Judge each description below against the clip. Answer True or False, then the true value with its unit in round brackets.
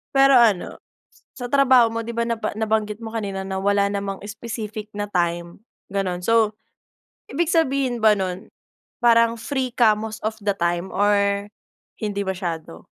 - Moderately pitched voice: False (215 Hz)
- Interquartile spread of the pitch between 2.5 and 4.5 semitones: True (2.8 semitones)